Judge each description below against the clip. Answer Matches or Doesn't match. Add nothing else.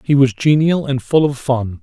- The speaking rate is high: Matches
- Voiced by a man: Matches